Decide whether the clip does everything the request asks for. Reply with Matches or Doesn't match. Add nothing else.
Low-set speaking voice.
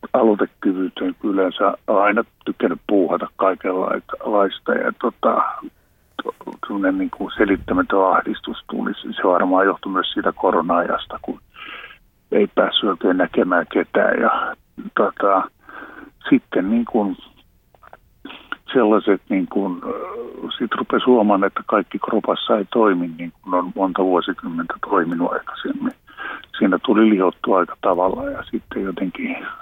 Doesn't match